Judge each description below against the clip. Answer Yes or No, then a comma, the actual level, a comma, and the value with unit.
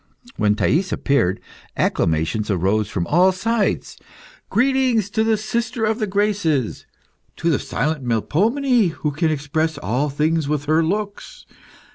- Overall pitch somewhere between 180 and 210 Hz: No, medium, 160 Hz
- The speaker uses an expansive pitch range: Yes, wide, 7.7 semitones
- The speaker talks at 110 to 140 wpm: Yes, slow, 135 wpm